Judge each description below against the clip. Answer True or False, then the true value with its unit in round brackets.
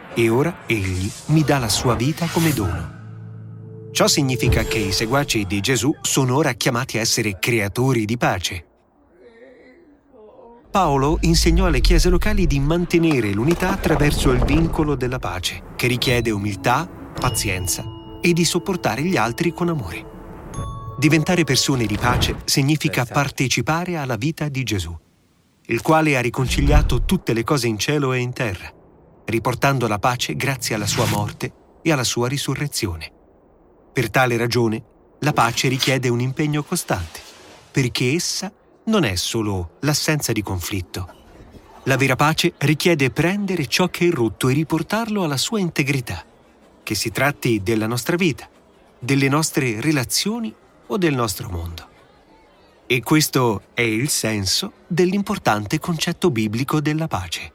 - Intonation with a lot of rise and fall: True (6.2 semitones)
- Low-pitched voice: True (130 Hz)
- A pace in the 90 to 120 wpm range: False (140 wpm)